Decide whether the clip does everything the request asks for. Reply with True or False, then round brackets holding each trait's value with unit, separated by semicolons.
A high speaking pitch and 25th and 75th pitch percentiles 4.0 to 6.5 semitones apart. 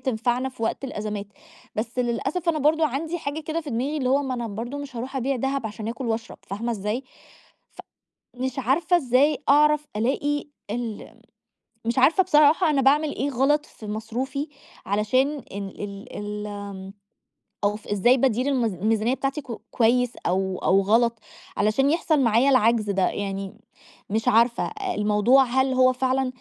True (250 Hz; 4.4 semitones)